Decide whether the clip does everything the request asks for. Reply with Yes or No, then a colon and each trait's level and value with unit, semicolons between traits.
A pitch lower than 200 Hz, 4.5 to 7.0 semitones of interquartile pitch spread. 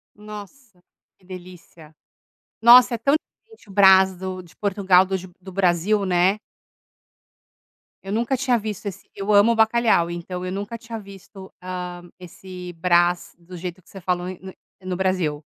No: high, 190 Hz; average, 2.7 semitones